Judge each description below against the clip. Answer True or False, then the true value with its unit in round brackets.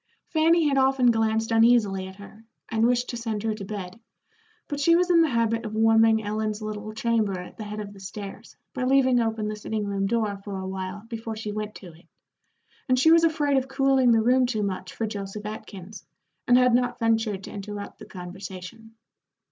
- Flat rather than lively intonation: False (3.2 semitones)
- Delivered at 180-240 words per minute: True (205 wpm)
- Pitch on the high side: True (220 Hz)